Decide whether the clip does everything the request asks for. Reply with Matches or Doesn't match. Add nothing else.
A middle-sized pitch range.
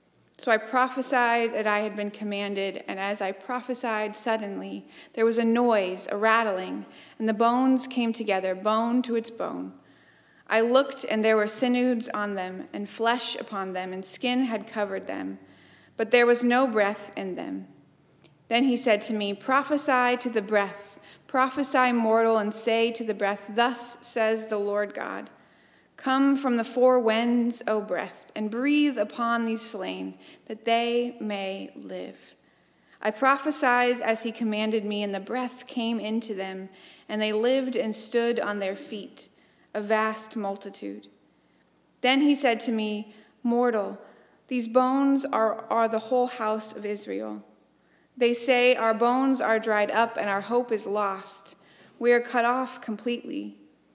Matches